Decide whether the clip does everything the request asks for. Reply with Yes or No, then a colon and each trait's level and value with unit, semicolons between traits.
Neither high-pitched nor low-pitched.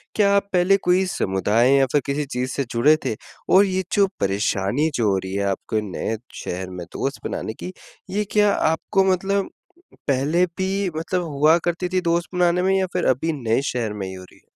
Yes: medium, 150 Hz